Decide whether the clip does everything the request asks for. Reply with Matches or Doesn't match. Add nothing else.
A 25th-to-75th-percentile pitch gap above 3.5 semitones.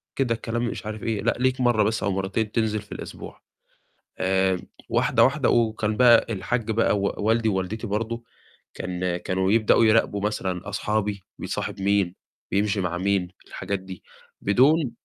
Doesn't match